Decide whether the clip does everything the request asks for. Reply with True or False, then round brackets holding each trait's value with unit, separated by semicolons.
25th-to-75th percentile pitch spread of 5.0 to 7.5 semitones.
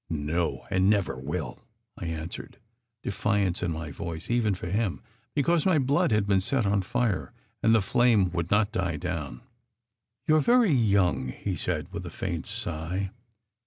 True (5.3 semitones)